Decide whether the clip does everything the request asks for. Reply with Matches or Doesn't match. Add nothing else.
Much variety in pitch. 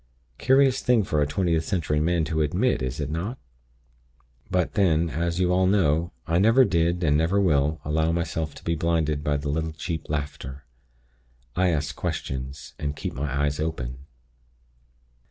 Doesn't match